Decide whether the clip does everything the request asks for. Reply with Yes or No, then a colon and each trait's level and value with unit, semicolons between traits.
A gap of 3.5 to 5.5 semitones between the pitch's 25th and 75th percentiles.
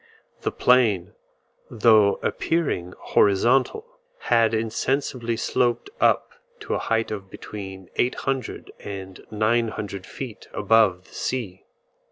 Yes: average, 3.8 semitones